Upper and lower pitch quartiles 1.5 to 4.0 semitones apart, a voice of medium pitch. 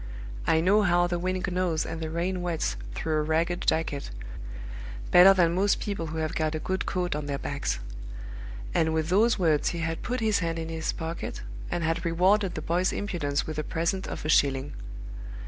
Yes: narrow, 2.6 semitones; medium, 165 Hz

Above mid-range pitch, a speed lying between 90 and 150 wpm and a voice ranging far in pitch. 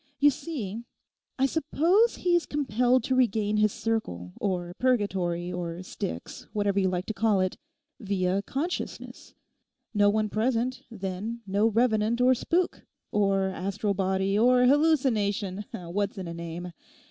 No: high, 210 Hz; average, 140 wpm; average, 4.8 semitones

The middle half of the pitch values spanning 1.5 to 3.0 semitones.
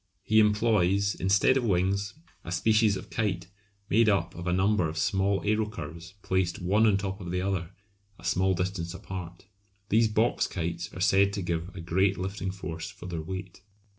Yes: narrow, 2.5 semitones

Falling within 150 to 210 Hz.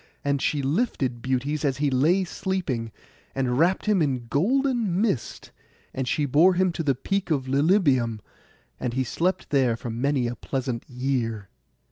No: medium, 140 Hz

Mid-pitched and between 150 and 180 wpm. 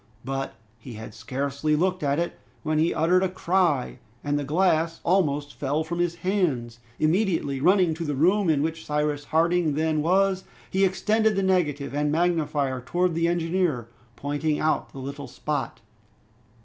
Yes: medium, 160 Hz; average, 160 wpm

